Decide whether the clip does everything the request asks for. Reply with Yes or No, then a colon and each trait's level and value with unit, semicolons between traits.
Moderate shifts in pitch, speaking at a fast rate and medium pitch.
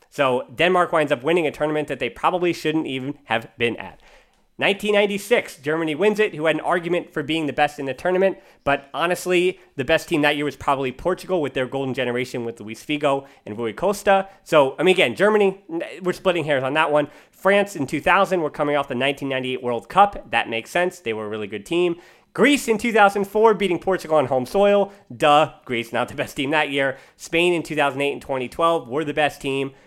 Yes: average, 4.9 semitones; fast, 210 wpm; medium, 155 Hz